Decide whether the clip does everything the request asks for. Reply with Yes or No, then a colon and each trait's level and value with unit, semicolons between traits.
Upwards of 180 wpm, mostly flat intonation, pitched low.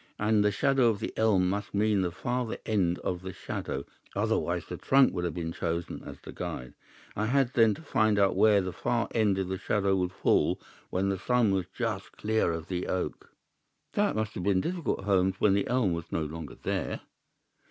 No: fast, 205 wpm; average, 3.3 semitones; low, 100 Hz